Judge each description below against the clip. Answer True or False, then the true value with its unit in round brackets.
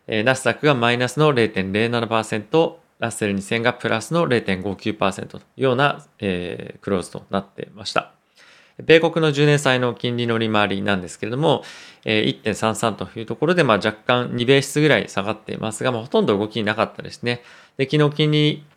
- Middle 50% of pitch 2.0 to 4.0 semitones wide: False (5.3 semitones)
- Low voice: True (120 Hz)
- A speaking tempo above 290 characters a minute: True (330 characters per minute)